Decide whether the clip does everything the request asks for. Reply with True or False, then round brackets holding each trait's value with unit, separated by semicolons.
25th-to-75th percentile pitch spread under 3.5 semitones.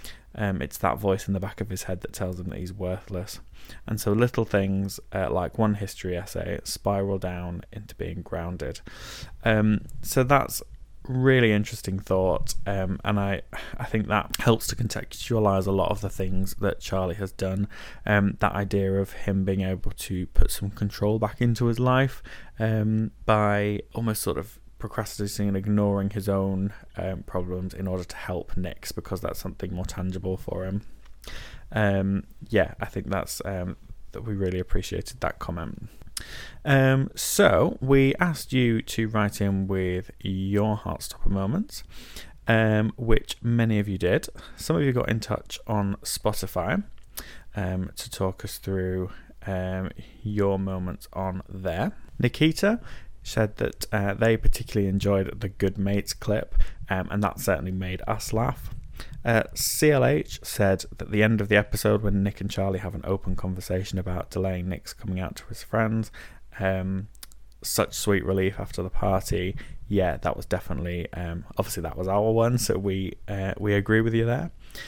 True (2.6 semitones)